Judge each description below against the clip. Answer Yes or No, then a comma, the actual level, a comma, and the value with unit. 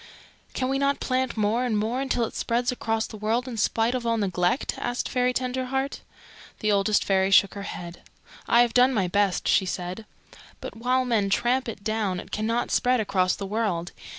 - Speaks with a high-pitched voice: Yes, high, 225 Hz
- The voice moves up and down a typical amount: Yes, average, 3.8 semitones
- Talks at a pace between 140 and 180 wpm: No, average, 195 wpm